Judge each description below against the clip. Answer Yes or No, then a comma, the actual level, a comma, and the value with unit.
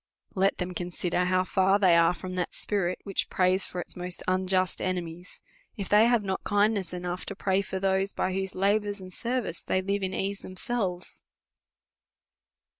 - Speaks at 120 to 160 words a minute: No, average, 180 wpm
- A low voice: No, medium, 185 Hz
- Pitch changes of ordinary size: No, narrow, 1.6 semitones